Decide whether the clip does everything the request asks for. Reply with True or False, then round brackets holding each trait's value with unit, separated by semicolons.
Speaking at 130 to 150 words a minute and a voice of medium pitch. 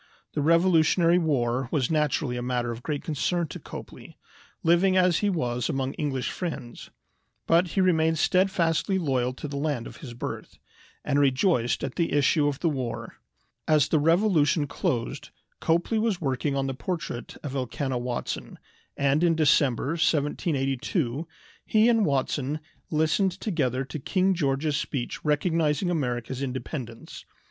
True (145 wpm; 150 Hz)